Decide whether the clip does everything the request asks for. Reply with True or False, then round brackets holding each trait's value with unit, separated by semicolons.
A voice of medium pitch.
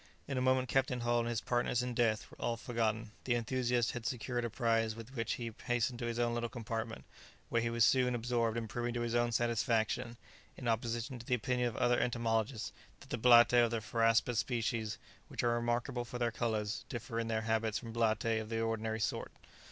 False (120 Hz)